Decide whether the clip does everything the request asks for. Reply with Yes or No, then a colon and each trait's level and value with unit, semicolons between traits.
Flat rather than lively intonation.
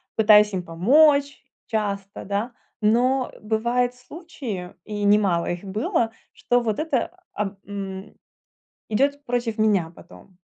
No: average, 3.8 semitones